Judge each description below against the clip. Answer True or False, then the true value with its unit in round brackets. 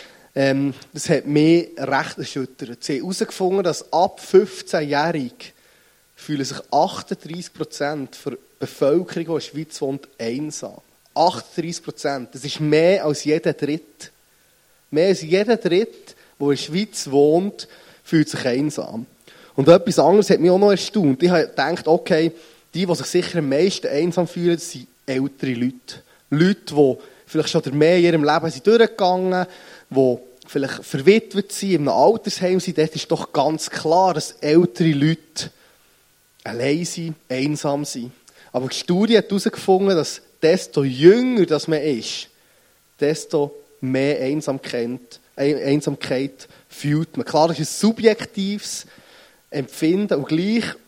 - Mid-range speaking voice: True (160 Hz)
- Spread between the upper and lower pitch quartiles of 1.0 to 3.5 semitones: False (4.1 semitones)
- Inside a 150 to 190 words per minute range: False (140 wpm)